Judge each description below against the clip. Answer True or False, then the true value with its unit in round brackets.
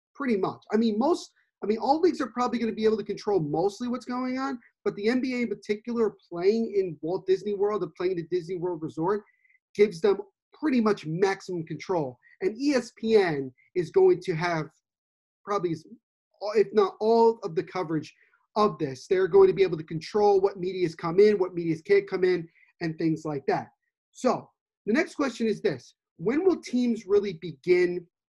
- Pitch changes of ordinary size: False (5.7 semitones)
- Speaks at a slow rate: False (190 wpm)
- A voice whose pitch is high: True (205 Hz)